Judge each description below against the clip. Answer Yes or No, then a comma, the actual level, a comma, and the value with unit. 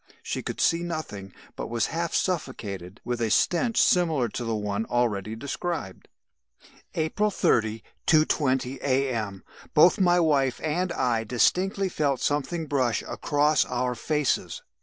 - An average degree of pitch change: No, wide, 6.2 semitones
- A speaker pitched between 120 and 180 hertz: Yes, low, 135 Hz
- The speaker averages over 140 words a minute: No, slow, 135 wpm